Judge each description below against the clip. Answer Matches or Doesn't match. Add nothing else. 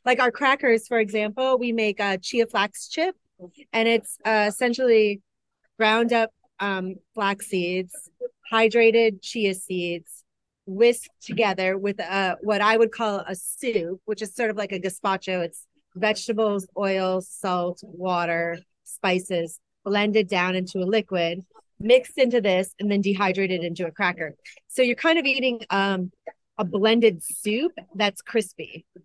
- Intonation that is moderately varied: Matches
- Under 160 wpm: Matches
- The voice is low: Doesn't match